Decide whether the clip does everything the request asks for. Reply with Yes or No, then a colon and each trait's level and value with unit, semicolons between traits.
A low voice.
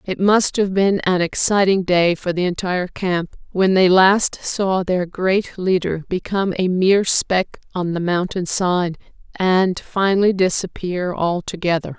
No: medium, 185 Hz